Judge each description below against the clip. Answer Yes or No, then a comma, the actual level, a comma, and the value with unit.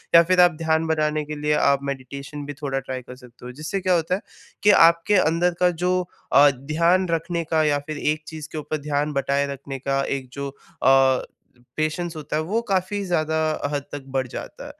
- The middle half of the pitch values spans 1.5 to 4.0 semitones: Yes, average, 3.4 semitones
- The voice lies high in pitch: No, medium, 155 Hz